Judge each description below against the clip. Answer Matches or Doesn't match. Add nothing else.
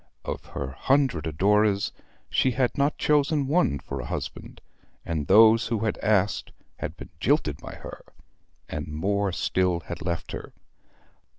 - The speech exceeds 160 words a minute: Doesn't match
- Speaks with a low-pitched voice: Matches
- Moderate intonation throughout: Doesn't match